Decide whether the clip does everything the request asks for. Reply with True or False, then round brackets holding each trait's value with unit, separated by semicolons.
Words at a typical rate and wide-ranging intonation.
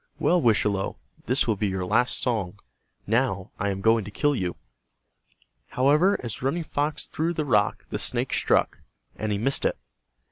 True (170 wpm; 6.0 semitones)